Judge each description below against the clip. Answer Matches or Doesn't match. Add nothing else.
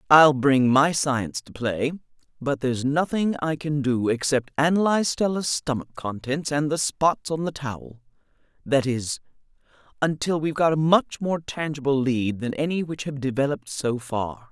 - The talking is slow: Doesn't match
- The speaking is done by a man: Doesn't match